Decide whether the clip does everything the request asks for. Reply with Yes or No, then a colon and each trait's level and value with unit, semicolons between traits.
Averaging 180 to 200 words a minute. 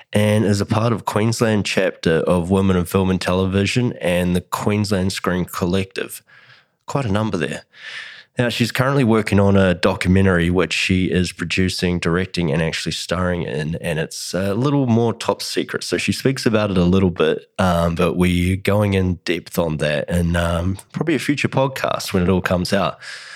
Yes: average, 185 wpm